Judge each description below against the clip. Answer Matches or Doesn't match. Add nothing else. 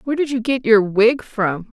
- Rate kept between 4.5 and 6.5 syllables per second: Matches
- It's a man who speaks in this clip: Doesn't match